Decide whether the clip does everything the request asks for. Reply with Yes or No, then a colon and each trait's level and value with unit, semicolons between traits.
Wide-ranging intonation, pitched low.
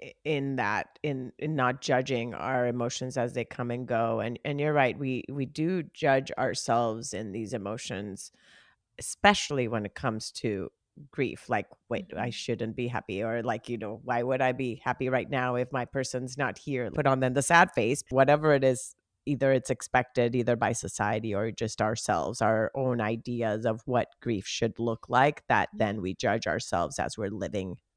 No: average, 2.7 semitones; low, 125 Hz